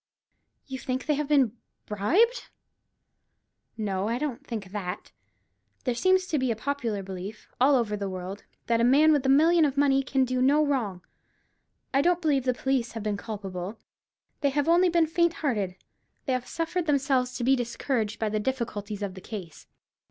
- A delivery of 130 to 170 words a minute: No, average, 180 wpm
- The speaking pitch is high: Yes, very high, 255 Hz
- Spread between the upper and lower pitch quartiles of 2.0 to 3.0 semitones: No, wide, 5.5 semitones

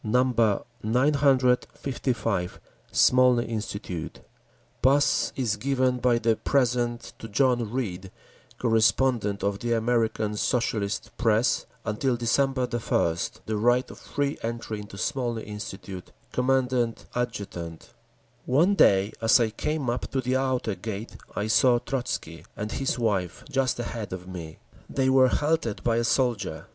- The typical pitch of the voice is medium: No, low, 120 Hz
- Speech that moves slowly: Yes, slow, 130 wpm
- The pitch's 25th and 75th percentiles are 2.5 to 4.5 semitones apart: Yes, average, 3.4 semitones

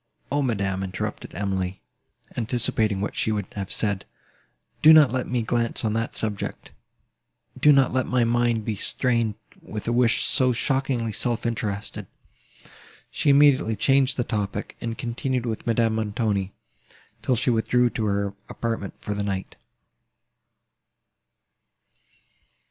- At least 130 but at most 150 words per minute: Yes, slow, 135 wpm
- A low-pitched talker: Yes, low, 115 Hz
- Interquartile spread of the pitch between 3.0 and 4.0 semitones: Yes, average, 3.3 semitones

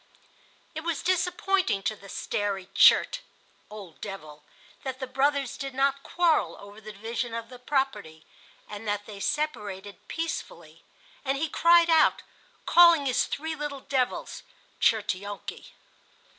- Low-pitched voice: No, very high, 260 Hz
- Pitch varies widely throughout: Yes, wide, 6.8 semitones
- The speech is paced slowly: Yes, slow, 130 wpm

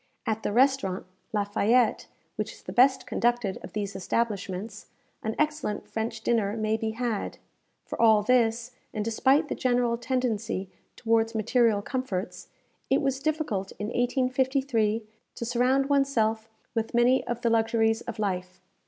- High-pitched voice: Yes, high, 230 Hz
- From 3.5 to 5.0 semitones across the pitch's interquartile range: No, average, 2.8 semitones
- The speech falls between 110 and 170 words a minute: Yes, average, 150 wpm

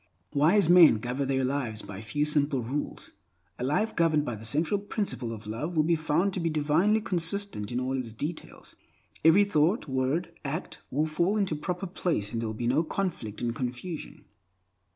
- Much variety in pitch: Yes, wide, 5.8 semitones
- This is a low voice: No, medium, 150 Hz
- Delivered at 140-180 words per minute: No, average, 190 wpm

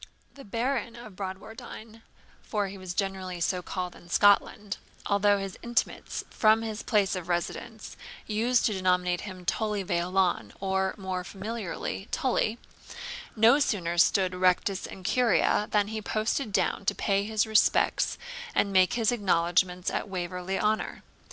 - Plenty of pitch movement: No, average, 2.9 semitones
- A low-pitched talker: No, high, 200 Hz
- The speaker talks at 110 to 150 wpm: Yes, average, 145 wpm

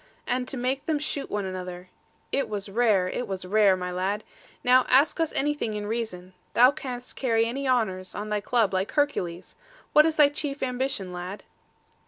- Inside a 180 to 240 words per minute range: Yes, average, 185 wpm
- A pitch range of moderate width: No, wide, 5.8 semitones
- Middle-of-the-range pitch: No, high, 225 Hz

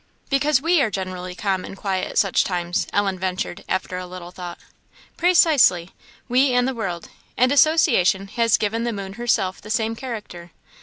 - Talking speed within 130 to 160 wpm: No, average, 170 wpm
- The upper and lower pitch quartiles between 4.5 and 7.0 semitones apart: Yes, average, 5.2 semitones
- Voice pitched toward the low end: No, high, 200 Hz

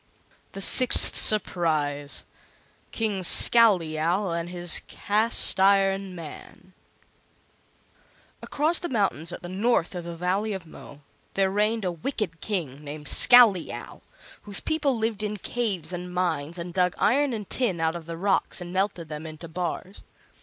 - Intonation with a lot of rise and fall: No, average, 4.1 semitones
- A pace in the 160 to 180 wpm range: No, average, 145 wpm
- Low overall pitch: No, medium, 185 Hz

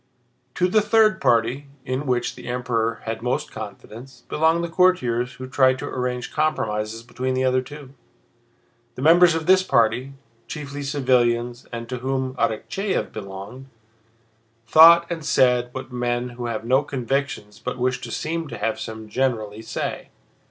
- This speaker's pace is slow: No, average, 150 wpm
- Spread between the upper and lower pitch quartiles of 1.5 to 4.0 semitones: Yes, average, 3.4 semitones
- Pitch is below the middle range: Yes, low, 130 Hz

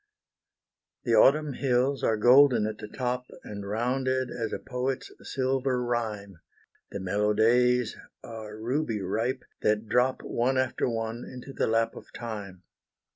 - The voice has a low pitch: Yes, low, 120 Hz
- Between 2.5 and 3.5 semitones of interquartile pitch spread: Yes, average, 3.2 semitones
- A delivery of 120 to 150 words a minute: Yes, average, 140 wpm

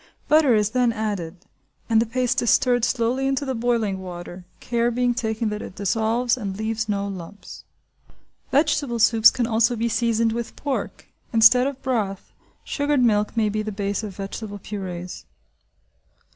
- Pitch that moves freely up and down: No, average, 3.0 semitones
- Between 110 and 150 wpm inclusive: No, average, 160 wpm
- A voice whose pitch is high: Yes, high, 225 Hz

